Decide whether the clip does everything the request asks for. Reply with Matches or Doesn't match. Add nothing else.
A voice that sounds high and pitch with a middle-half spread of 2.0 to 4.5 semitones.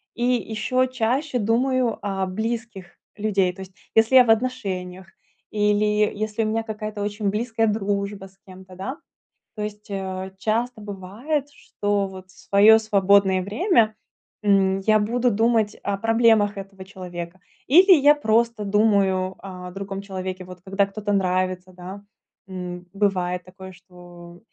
Matches